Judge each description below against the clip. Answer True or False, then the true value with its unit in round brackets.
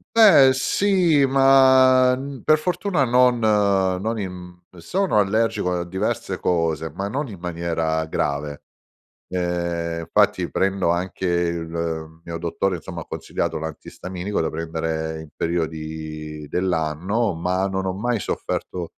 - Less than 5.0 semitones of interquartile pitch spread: False (6.1 semitones)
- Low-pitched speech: True (90 Hz)